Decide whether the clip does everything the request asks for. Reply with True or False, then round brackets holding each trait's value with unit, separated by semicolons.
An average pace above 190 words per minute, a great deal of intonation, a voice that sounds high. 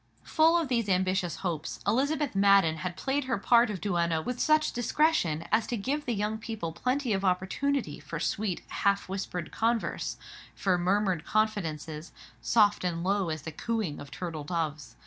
False (165 wpm; 5.7 semitones; 195 Hz)